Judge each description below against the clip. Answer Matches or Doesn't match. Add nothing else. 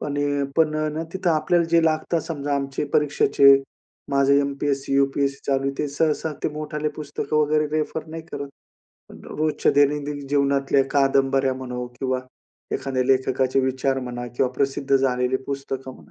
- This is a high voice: Doesn't match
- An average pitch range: Doesn't match